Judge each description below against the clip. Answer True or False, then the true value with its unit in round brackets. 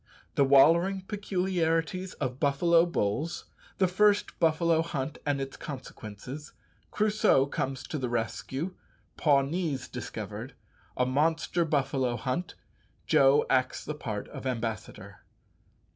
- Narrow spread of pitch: False (4.6 semitones)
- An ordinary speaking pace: False (115 wpm)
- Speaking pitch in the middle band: True (145 Hz)